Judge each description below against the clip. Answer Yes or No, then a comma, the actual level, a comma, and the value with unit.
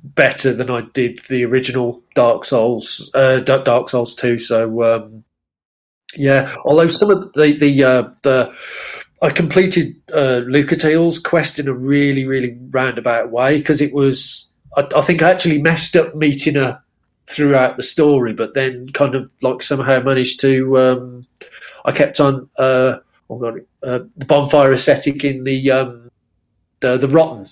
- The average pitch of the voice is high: No, low, 135 Hz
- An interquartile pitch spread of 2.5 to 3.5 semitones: Yes, average, 2.8 semitones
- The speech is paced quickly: No, average, 165 wpm